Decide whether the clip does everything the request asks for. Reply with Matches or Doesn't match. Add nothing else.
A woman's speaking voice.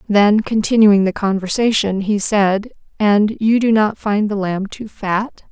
Matches